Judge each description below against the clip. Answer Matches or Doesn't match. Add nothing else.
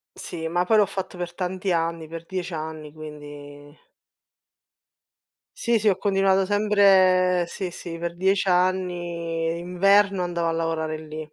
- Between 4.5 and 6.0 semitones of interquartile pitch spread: Doesn't match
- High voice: Doesn't match